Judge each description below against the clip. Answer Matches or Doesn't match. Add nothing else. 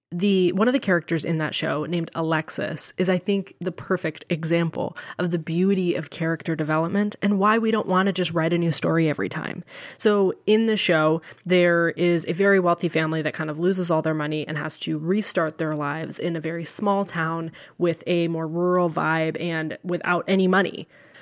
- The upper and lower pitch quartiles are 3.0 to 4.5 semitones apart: Doesn't match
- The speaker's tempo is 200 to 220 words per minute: Matches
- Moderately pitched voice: Matches